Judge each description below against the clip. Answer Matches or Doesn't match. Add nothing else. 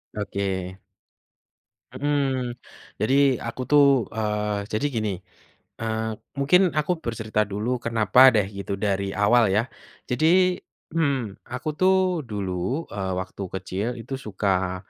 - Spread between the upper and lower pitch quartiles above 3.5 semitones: Matches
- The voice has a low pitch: Matches